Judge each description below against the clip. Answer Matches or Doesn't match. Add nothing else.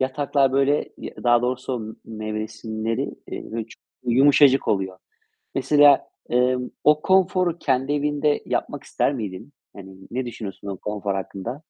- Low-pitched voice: Matches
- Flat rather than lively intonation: Doesn't match